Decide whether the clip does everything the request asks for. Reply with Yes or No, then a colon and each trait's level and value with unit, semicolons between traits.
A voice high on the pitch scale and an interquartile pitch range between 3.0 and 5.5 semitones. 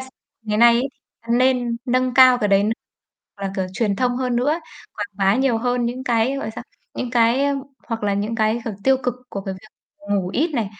Yes: high, 235 Hz; average, 3.5 semitones